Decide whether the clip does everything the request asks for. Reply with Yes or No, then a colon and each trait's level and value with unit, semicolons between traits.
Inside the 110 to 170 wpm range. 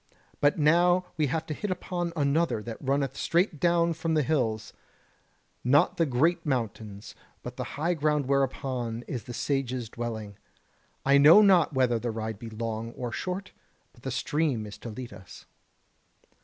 Yes: average, 165 wpm